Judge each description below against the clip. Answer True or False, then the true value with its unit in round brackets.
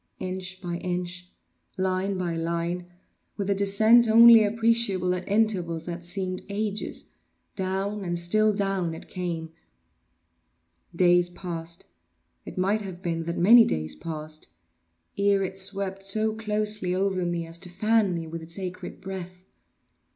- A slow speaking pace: True (125 wpm)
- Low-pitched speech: False (185 Hz)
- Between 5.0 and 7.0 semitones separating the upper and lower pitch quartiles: False (2.8 semitones)